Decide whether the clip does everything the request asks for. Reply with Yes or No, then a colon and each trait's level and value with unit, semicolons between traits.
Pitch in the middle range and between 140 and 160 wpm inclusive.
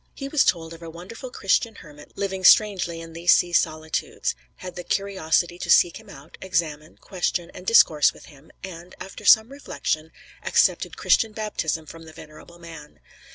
No: medium, 175 Hz; average, 170 wpm